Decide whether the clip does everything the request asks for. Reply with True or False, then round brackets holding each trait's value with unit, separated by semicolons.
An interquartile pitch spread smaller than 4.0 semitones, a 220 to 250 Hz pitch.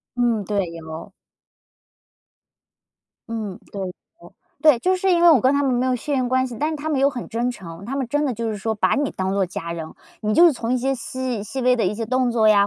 False (4.4 semitones; 240 Hz)